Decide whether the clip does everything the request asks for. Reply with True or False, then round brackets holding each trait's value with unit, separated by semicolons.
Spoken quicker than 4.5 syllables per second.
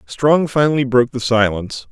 True (5.7 syllables/s)